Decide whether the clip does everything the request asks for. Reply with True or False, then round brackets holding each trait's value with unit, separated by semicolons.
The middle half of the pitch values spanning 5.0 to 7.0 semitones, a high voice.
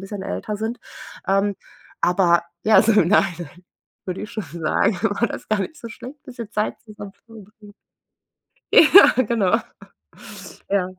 False (2.8 semitones; 205 Hz)